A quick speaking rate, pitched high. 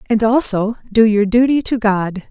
No: average, 180 wpm; high, 220 Hz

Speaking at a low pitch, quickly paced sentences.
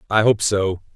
No: low, 105 Hz; average, 190 wpm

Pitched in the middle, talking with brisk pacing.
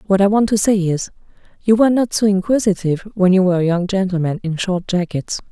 No: high, 195 Hz; fast, 220 wpm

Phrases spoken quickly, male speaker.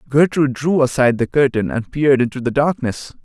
No: average, 185 wpm; male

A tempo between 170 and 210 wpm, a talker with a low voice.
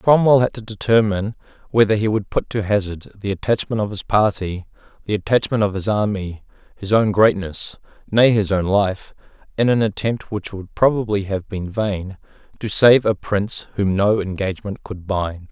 Yes: average, 175 wpm; low, 105 Hz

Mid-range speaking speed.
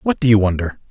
No: fast, 265 wpm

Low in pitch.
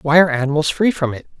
No: medium, 150 Hz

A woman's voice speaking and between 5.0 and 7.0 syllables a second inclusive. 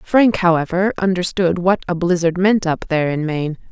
Yes: female; 5.3 syllables/s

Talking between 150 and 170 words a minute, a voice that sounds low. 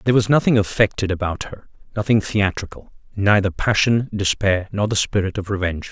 Yes: average, 160 wpm; low, 100 Hz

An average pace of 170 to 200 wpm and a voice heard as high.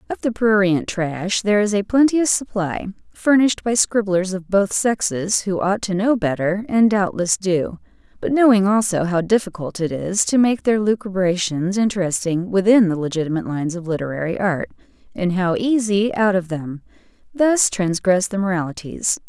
No: average, 160 wpm; high, 195 Hz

